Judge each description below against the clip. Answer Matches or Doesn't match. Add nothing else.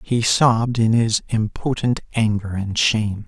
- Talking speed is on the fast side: Doesn't match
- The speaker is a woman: Doesn't match